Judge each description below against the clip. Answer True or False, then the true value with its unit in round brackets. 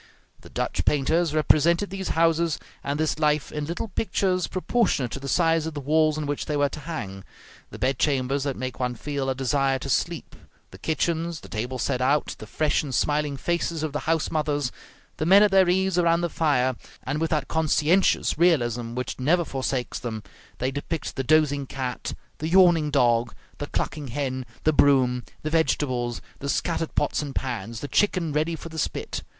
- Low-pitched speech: False (150 Hz)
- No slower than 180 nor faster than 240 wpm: True (190 wpm)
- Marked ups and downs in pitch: False (3.7 semitones)